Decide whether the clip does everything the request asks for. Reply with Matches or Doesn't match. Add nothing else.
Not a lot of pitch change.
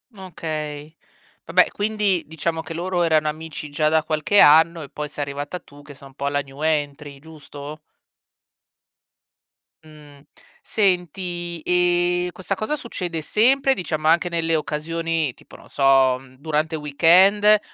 Doesn't match